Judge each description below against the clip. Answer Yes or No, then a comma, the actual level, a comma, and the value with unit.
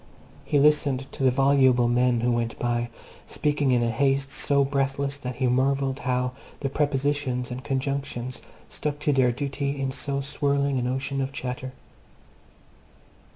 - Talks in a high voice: No, low, 135 Hz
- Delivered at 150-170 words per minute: Yes, average, 155 wpm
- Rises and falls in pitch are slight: Yes, narrow, 1.9 semitones